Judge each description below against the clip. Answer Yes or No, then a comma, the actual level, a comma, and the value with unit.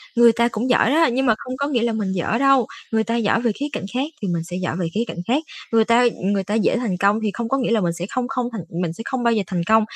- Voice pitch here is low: No, high, 225 Hz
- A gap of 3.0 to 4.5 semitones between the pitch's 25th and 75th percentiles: Yes, average, 3.6 semitones